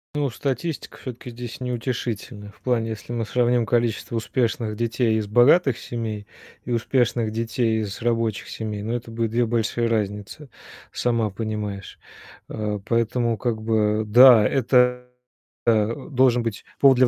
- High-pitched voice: No, low, 115 Hz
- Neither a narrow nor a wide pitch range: No, narrow, 2.1 semitones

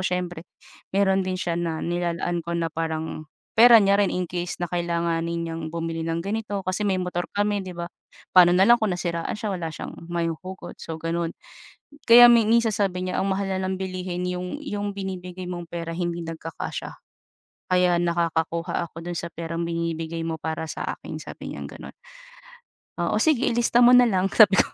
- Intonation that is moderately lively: No, narrow, 2.3 semitones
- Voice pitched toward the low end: No, medium, 175 Hz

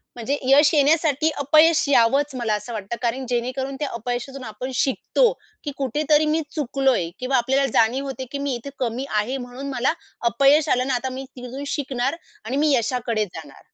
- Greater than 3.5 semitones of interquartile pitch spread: No, average, 2.7 semitones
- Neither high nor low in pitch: No, very high, 265 Hz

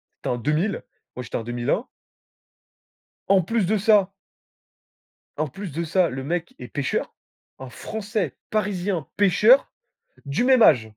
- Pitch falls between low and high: Yes, medium, 180 Hz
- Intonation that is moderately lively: No, wide, 6.9 semitones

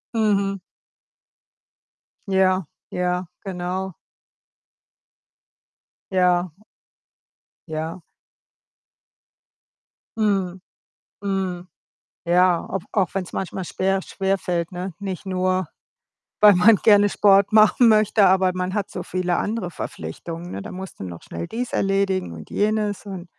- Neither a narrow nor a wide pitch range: No, narrow, 1.8 semitones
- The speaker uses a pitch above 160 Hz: Yes, high, 190 Hz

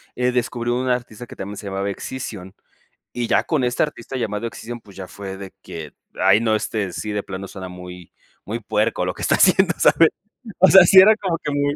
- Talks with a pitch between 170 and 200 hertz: No, low, 110 Hz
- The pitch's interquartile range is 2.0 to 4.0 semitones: No, average, 4.8 semitones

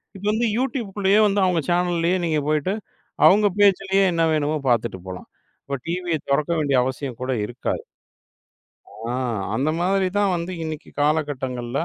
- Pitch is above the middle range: No, medium, 165 Hz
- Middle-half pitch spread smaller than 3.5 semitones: No, wide, 5.5 semitones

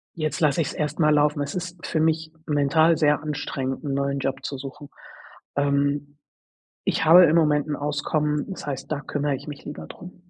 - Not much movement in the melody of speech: Yes, narrow, 1.8 semitones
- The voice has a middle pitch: Yes, medium, 150 Hz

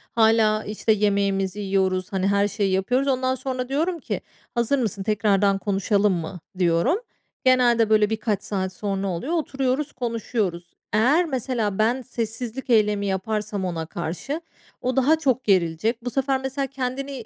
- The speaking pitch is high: Yes, high, 220 Hz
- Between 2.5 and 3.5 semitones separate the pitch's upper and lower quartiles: No, average, 4.7 semitones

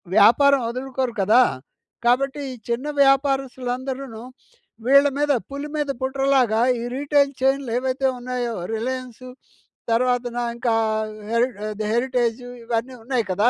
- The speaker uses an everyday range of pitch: No, narrow, 2.3 semitones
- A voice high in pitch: Yes, very high, 255 Hz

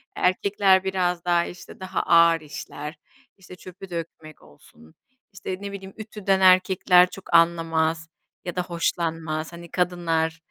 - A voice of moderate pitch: Yes, medium, 175 Hz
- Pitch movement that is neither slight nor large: No, narrow, 2.3 semitones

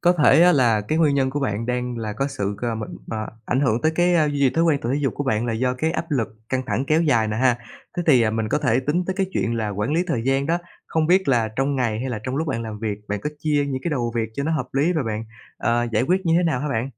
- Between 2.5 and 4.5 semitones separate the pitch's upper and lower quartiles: No, average, 5.1 semitones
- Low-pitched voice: Yes, low, 130 Hz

